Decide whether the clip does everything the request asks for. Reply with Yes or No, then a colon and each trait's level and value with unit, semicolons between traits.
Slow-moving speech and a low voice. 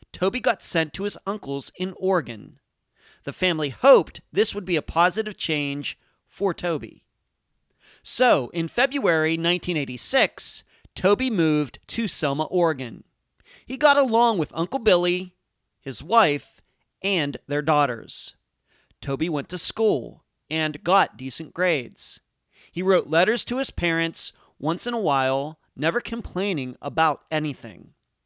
No: slow, 130 wpm; medium, 165 Hz